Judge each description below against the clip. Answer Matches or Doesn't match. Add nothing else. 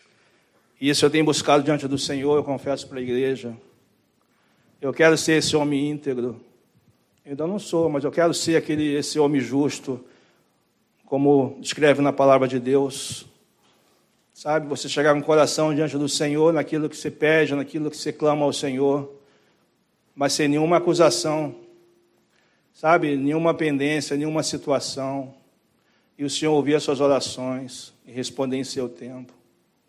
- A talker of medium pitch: Matches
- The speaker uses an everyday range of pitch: Doesn't match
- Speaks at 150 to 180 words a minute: Matches